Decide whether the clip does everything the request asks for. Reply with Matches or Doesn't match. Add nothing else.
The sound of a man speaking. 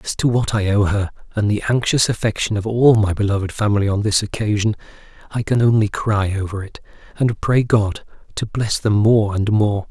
Matches